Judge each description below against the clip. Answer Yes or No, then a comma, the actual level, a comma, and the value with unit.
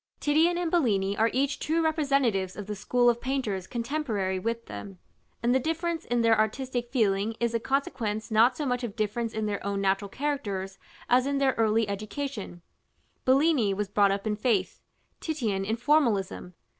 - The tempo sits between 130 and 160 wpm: No, average, 175 wpm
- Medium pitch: No, high, 230 Hz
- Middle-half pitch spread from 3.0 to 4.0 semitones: No, average, 5.2 semitones